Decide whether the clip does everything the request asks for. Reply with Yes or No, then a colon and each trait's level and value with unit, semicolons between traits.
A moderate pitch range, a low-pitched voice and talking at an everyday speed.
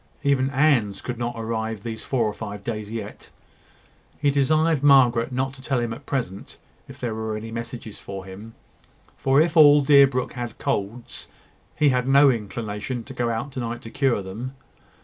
Yes: average, 3.5 semitones; low, 120 Hz; average, 180 wpm